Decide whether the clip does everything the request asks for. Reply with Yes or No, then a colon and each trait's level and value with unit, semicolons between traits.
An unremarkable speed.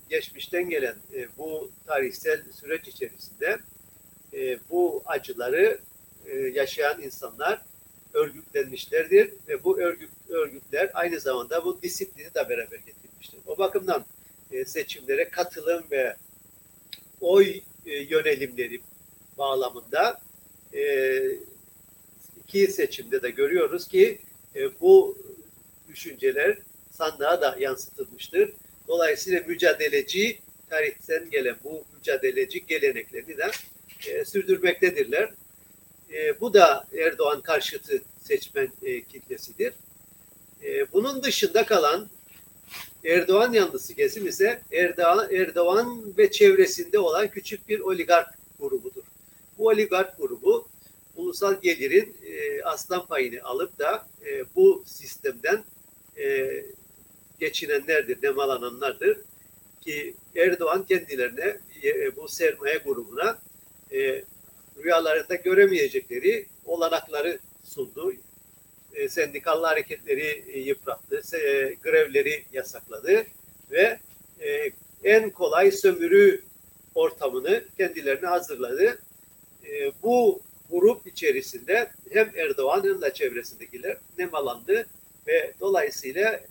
No: slow, 85 wpm